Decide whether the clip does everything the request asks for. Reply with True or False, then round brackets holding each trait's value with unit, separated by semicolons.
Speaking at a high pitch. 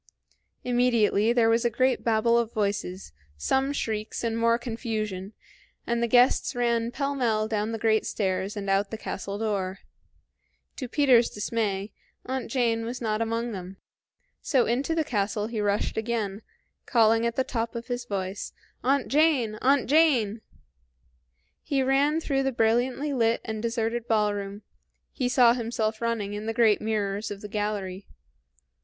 True (225 Hz)